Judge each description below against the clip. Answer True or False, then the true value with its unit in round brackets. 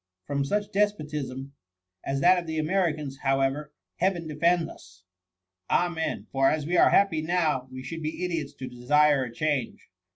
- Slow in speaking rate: False (165 wpm)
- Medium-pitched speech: True (150 Hz)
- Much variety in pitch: False (4.0 semitones)